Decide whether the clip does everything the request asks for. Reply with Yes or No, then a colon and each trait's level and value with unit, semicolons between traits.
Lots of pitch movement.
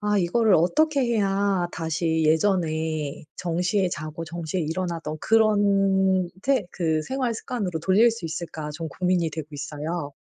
No: average, 4.0 semitones